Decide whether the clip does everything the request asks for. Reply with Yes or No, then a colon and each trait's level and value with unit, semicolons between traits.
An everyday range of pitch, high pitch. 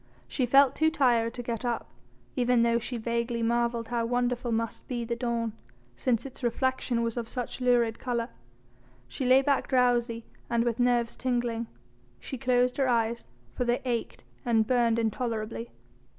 No: narrow, 1.2 semitones; high, 240 Hz